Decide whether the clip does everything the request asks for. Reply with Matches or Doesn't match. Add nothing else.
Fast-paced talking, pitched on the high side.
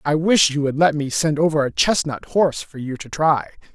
Doesn't match